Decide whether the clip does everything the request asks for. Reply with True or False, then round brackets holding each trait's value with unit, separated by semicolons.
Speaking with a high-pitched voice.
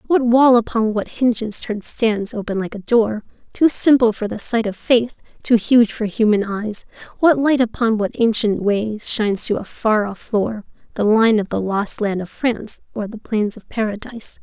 True (220 Hz)